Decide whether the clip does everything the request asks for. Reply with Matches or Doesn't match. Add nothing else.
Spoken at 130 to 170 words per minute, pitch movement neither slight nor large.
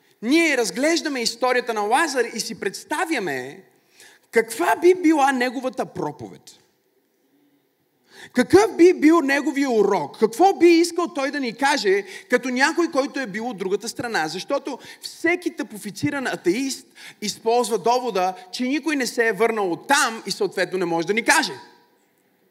Doesn't match